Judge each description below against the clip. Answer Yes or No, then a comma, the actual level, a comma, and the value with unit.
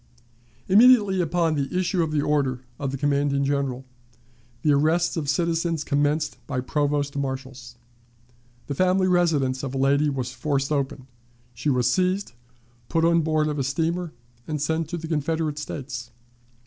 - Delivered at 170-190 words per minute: No, average, 155 wpm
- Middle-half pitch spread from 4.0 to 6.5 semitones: No, average, 3.1 semitones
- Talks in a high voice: No, medium, 150 Hz